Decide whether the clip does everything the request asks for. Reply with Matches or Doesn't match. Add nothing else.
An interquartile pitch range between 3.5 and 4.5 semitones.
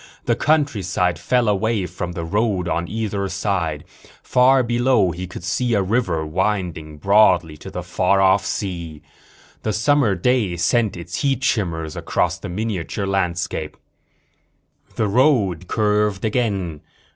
Matches